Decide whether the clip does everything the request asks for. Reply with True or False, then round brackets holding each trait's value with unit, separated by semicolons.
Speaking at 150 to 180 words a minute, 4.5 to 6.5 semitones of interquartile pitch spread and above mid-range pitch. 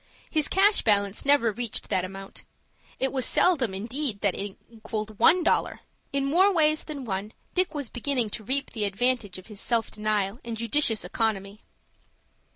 True (165 wpm; 5.3 semitones; 230 Hz)